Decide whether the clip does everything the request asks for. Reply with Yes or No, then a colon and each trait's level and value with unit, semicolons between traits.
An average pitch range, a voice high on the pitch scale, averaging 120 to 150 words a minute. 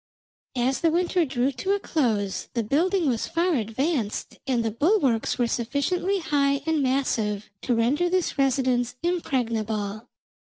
No: wide, 6.3 semitones; very high, 265 Hz; average, 145 wpm